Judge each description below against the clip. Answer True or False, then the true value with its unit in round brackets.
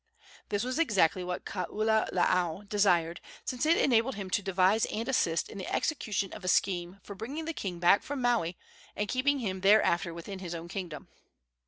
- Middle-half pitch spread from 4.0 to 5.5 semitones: True (4.4 semitones)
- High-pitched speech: True (195 Hz)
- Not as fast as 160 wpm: False (180 wpm)